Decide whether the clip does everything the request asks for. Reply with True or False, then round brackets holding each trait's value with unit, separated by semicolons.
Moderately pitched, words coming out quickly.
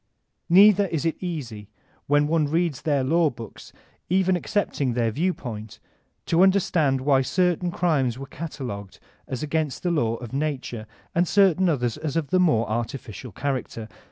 False (145 Hz; 160 wpm)